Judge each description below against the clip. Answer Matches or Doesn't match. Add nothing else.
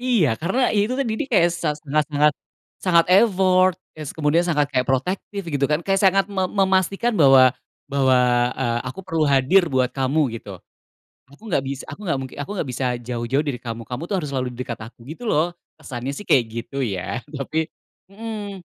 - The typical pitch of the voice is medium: Matches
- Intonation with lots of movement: Matches